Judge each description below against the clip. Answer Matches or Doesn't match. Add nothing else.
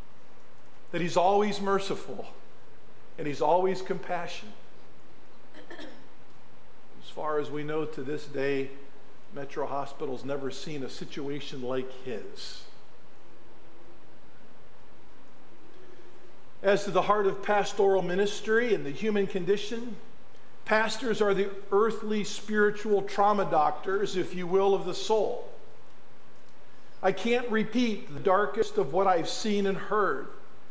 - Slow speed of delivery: Matches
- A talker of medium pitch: Doesn't match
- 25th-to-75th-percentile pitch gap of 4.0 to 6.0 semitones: Matches